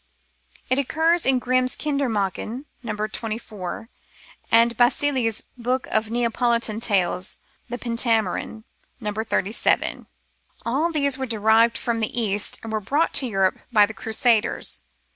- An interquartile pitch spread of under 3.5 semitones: Yes, average, 2.9 semitones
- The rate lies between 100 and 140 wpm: Yes, slow, 135 wpm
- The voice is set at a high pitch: Yes, high, 230 Hz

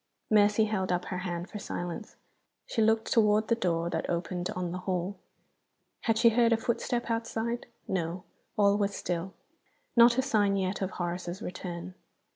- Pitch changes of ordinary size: Yes, average, 3.8 semitones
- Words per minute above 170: No, average, 165 wpm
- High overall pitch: Yes, high, 200 Hz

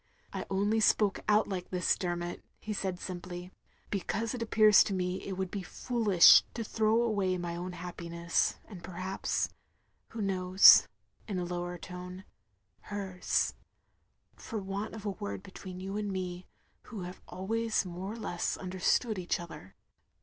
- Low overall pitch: No, high, 190 Hz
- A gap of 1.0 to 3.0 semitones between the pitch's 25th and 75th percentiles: Yes, narrow, 2.6 semitones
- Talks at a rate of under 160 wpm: No, average, 165 wpm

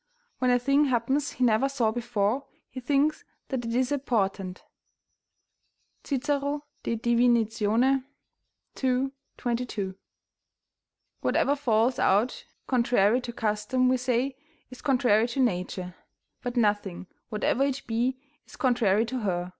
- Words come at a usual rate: No, slow, 125 wpm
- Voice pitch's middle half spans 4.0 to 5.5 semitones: No, average, 3.2 semitones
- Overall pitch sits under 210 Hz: No, high, 245 Hz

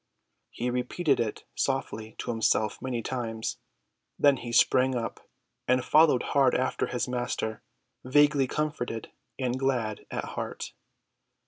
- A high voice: No, low, 125 Hz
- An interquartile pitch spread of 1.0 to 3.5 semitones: Yes, narrow, 2.6 semitones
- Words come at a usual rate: No, slow, 125 wpm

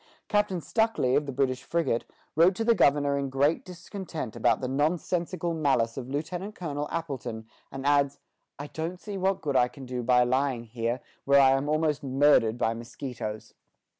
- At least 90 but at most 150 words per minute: No, average, 175 wpm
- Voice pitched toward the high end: No, medium, 140 Hz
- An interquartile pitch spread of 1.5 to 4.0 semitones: No, average, 4.6 semitones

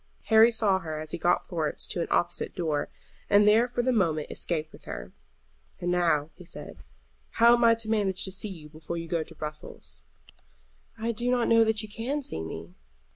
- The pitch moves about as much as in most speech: No, wide, 6.3 semitones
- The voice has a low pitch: No, medium, 185 Hz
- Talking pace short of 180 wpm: No, fast, 205 wpm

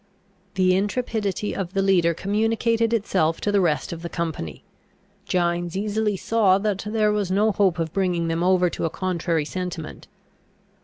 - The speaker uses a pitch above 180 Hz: Yes, high, 190 Hz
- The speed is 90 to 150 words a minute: No, average, 160 wpm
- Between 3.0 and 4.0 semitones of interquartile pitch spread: Yes, average, 3.4 semitones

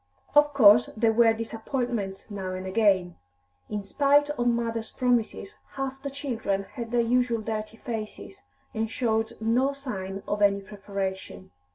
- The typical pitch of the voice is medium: No, high, 225 Hz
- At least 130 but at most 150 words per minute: Yes, average, 145 wpm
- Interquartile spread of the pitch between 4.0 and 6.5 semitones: No, average, 3.5 semitones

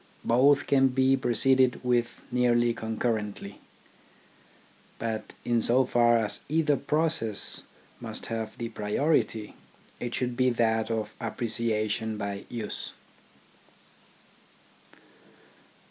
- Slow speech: Yes, slow, 100 wpm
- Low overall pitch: Yes, low, 120 Hz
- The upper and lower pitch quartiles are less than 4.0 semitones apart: Yes, narrow, 2.4 semitones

